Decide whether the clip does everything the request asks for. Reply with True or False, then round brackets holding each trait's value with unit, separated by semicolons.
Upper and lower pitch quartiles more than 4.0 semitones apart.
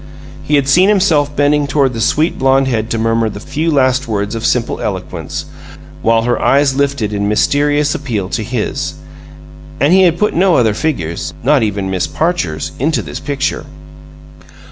True (4.8 semitones)